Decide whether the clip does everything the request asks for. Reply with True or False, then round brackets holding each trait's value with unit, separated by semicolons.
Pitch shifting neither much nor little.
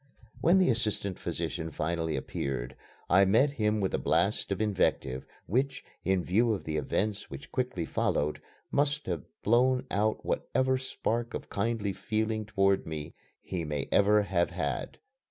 False (5.7 semitones)